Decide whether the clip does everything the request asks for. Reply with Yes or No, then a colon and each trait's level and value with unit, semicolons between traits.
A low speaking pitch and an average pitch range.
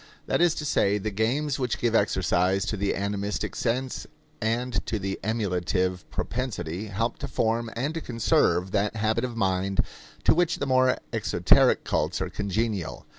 Yes: low, 110 Hz; average, 4.1 semitones